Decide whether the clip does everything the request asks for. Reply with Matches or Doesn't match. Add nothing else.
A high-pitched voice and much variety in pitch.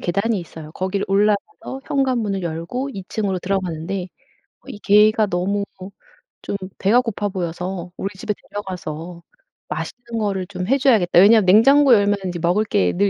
Doesn't match